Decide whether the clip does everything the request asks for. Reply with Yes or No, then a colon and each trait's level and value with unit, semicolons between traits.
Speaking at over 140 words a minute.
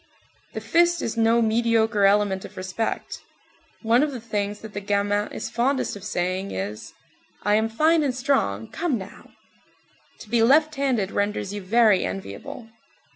Yes: average, 160 wpm